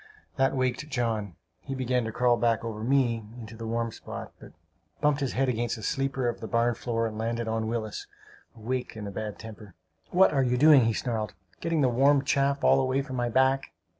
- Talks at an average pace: No, fast, 210 wpm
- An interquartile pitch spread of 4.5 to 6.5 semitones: No, average, 3.0 semitones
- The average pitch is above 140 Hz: No, low, 120 Hz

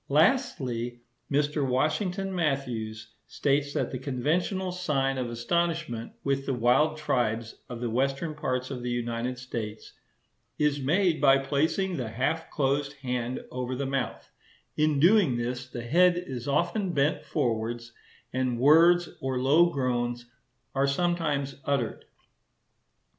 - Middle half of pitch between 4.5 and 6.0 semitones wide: No, average, 4.0 semitones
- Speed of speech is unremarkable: No, slow, 130 wpm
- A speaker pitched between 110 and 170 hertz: Yes, low, 135 Hz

